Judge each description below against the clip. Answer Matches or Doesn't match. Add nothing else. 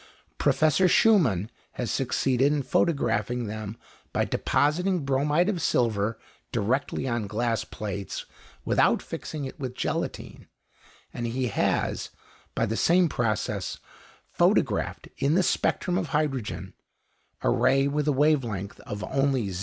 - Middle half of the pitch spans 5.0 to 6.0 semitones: Matches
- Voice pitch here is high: Doesn't match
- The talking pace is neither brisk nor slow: Doesn't match